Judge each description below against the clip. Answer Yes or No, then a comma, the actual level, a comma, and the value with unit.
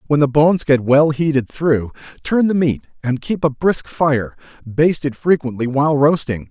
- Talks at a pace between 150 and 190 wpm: Yes, average, 175 wpm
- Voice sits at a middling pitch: Yes, medium, 145 Hz